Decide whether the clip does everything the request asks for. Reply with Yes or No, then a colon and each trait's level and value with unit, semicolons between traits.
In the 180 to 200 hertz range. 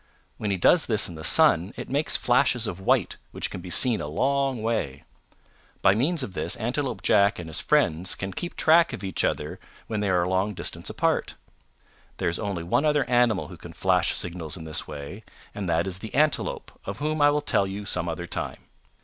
No: low, 100 Hz